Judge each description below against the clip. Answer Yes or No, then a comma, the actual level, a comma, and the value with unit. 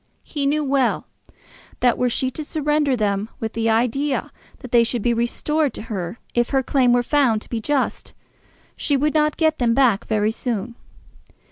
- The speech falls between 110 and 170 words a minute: No, average, 180 wpm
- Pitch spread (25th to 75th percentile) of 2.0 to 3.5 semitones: No, average, 3.9 semitones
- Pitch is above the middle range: Yes, very high, 250 Hz